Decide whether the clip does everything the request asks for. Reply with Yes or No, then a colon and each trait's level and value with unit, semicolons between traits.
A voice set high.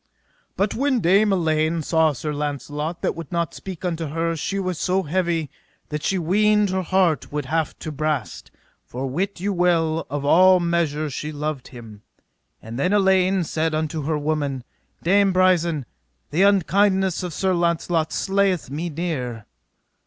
No: medium, 165 Hz